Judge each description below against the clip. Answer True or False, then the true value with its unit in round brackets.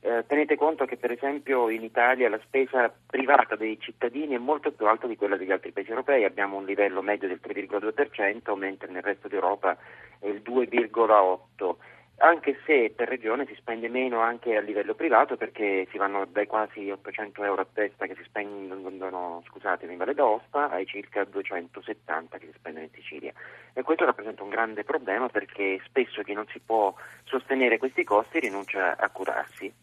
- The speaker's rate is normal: False (180 wpm)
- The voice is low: True (105 Hz)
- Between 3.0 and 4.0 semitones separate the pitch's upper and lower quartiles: True (3.5 semitones)